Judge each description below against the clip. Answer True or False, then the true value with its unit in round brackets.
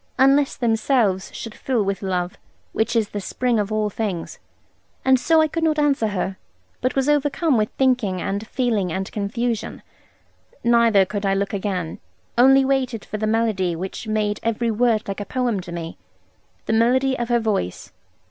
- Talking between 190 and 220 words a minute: False (175 wpm)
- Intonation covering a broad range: False (4.3 semitones)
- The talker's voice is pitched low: False (220 Hz)